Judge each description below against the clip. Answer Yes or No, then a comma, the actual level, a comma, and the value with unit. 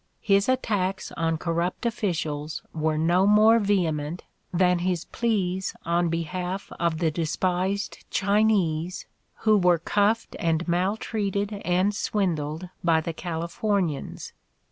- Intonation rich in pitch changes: No, average, 3.4 semitones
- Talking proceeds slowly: Yes, slow, 115 wpm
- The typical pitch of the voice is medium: Yes, medium, 180 Hz